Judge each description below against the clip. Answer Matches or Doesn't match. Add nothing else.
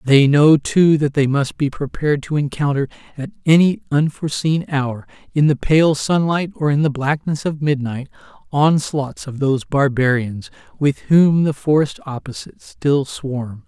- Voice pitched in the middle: Matches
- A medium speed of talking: Matches